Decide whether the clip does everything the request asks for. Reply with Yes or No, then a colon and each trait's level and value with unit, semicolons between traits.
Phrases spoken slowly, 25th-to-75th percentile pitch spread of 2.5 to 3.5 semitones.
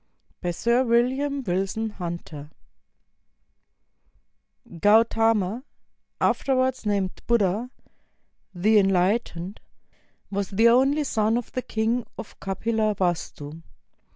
No: slow, 95 wpm; average, 3.9 semitones